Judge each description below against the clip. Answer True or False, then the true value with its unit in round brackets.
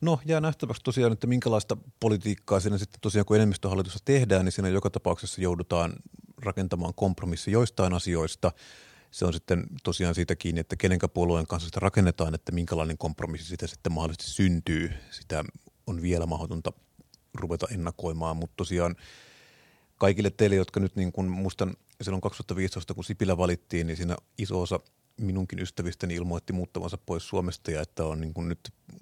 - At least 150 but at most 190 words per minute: True (155 wpm)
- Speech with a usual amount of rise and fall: True (3.0 semitones)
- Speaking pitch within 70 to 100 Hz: True (90 Hz)